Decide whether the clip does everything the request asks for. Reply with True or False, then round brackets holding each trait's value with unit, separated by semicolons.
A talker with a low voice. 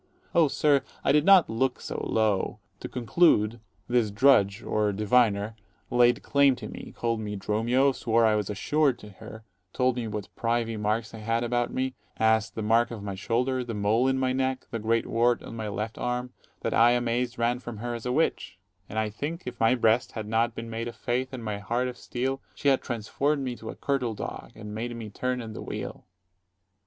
True (115 Hz)